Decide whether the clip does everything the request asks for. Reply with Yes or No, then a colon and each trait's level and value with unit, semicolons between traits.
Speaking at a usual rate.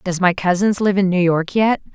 No: fast, 245 wpm